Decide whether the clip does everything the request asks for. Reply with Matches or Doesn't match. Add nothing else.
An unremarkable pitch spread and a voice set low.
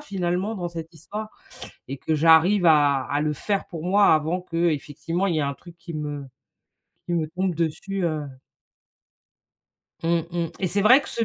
Doesn't match